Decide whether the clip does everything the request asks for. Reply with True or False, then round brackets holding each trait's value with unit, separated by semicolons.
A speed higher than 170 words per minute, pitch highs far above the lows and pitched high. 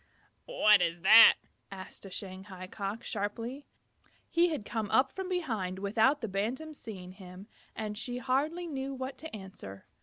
False (155 wpm; 5.7 semitones; 220 Hz)